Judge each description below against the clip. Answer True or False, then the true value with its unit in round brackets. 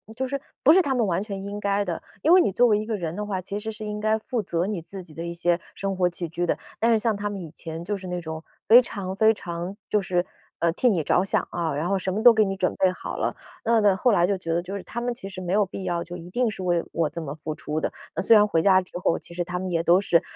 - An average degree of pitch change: True (3.4 semitones)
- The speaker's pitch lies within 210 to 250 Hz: False (190 Hz)